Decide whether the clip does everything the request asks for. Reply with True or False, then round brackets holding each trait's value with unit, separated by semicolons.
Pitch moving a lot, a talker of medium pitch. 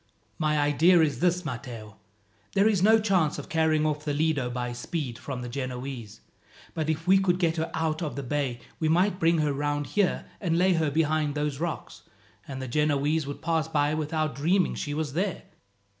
False (2.8 semitones; 155 Hz)